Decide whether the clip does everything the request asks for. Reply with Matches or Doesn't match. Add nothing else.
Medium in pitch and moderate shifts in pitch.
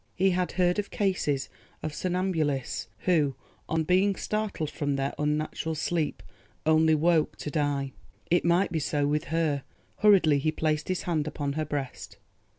Matches